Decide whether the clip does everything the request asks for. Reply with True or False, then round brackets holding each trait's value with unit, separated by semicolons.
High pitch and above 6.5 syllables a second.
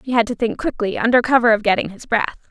True (230 Hz; 6.9 syllables/s)